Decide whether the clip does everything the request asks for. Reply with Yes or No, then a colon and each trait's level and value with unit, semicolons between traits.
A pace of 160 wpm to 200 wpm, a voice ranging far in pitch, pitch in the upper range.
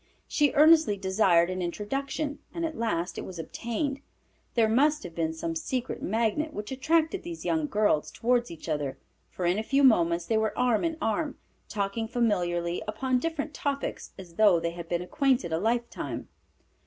Yes: average, 175 wpm; wide, 8.0 semitones; high, 225 Hz